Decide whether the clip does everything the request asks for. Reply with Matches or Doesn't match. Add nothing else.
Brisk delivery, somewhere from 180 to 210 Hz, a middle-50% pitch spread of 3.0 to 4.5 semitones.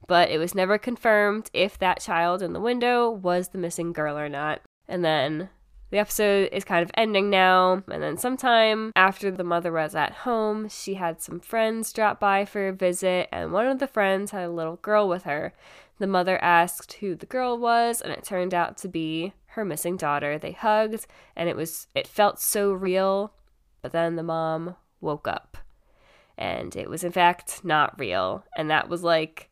Doesn't match